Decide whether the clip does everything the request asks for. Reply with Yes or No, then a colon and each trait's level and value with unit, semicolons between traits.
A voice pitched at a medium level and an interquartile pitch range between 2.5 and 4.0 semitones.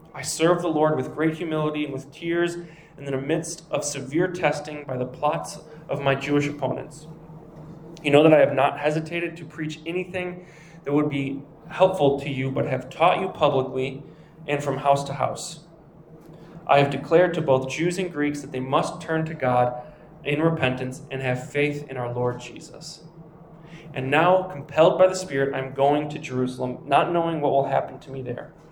Yes: medium, 150 Hz; average, 2.9 semitones